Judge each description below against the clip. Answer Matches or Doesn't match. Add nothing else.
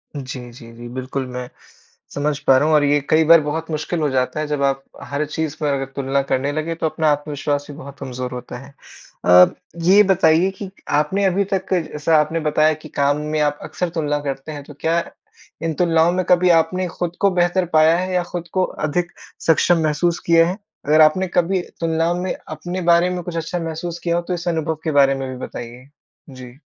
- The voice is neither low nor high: Matches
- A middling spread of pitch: Matches